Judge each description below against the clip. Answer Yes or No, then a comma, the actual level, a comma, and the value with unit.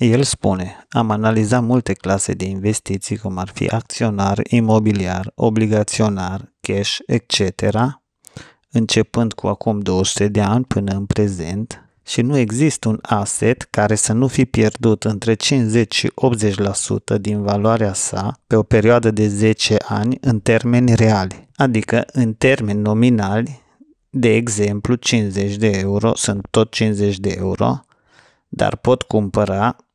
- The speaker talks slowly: No, average, 135 wpm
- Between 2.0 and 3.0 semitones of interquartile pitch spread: Yes, narrow, 2.6 semitones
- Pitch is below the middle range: Yes, low, 110 Hz